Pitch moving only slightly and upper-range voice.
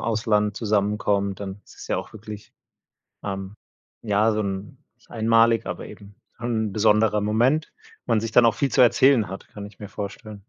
No: narrow, 2.0 semitones; low, 105 Hz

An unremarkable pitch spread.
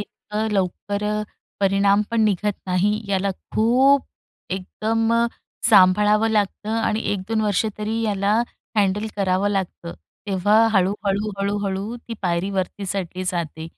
No: narrow, 2.0 semitones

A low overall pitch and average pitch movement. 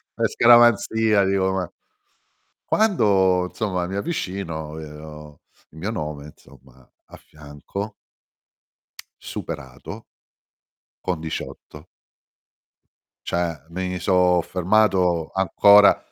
Yes: very low, 90 Hz; average, 4.2 semitones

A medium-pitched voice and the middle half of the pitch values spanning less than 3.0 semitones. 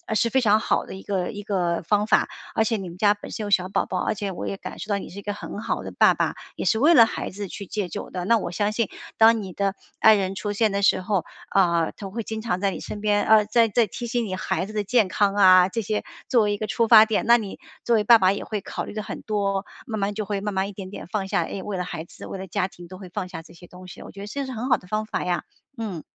No: high, 205 Hz; narrow, 2.5 semitones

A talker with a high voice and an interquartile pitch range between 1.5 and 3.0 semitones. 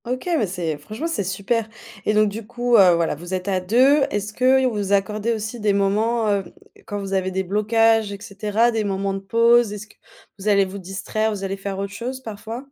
Yes: high, 210 Hz; average, 2.7 semitones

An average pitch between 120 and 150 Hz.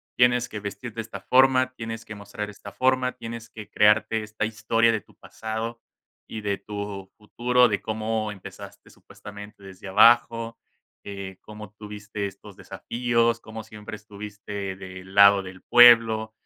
No: low, 110 Hz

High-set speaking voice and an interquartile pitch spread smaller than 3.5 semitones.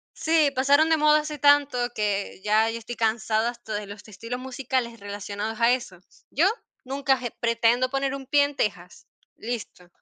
No: high, 240 Hz; average, 4.3 semitones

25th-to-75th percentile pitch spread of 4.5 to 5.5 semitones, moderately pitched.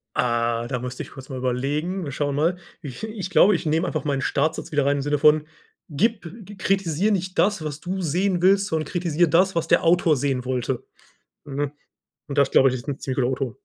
Yes: average, 5.0 semitones; medium, 150 Hz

